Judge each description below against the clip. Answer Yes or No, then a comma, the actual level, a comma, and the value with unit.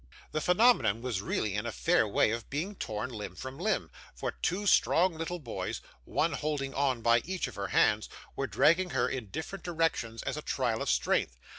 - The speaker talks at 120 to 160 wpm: No, average, 195 wpm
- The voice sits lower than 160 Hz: Yes, low, 135 Hz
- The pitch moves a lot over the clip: Yes, wide, 7.2 semitones